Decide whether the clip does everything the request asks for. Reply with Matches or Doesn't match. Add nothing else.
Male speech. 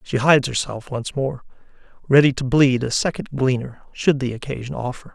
Matches